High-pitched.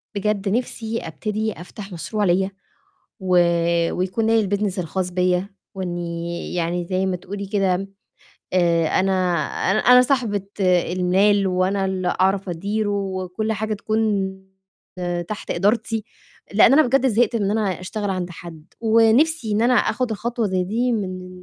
Yes: high, 195 Hz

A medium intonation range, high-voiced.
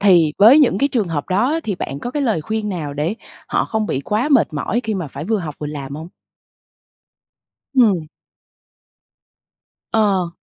No: wide, 6.3 semitones; high, 195 Hz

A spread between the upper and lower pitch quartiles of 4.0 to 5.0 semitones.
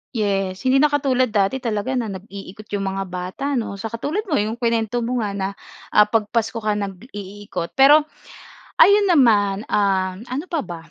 Yes: average, 4.4 semitones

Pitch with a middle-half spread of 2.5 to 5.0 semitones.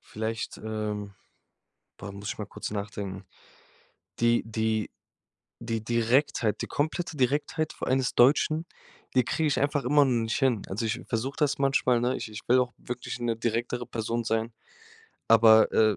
Yes: average, 2.9 semitones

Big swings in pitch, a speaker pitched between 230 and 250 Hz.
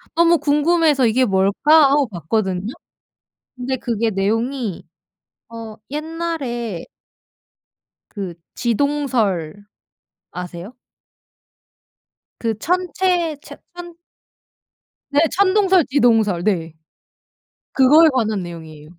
Yes: wide, 7.2 semitones; high, 240 Hz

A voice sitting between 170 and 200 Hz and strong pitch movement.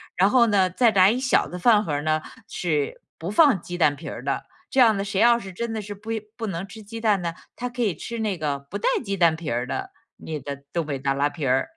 Yes: high, 190 Hz; wide, 6.2 semitones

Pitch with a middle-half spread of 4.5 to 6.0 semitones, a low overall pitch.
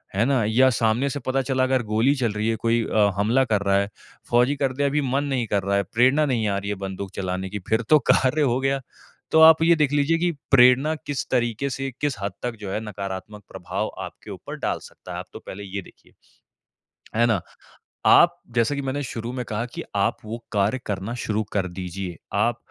Yes: average, 4.8 semitones; low, 115 Hz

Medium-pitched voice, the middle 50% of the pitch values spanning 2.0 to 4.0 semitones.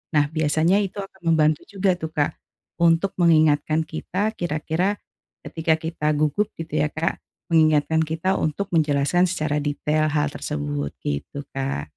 Yes: medium, 155 Hz; narrow, 2.5 semitones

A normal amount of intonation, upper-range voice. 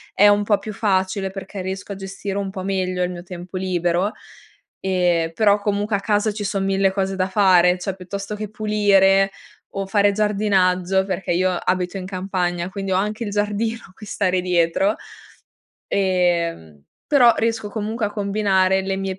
No: narrow, 1.9 semitones; high, 195 Hz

